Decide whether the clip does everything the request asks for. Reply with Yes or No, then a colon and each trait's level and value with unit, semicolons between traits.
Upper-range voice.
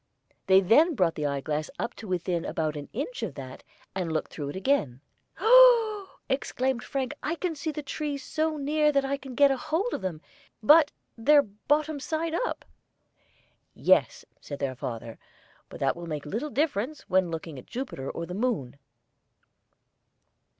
Yes: high, 245 Hz